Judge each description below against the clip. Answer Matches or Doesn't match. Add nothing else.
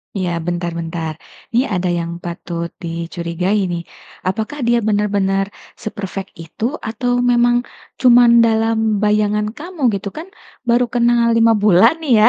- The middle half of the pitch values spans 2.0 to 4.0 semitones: Doesn't match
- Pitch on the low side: Doesn't match